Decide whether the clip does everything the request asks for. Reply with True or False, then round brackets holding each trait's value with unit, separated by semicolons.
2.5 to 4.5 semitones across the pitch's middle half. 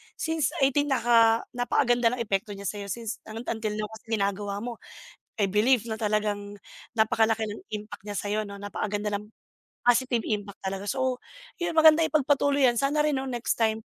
True (3.3 semitones)